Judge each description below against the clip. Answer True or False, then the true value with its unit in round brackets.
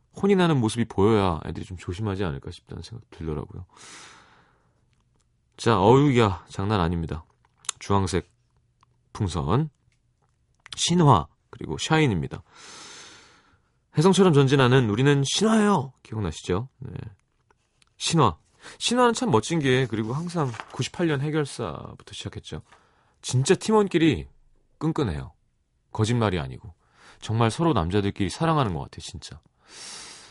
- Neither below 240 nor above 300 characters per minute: True (275 characters per minute)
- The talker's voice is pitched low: True (130 Hz)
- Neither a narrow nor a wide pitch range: False (7.5 semitones)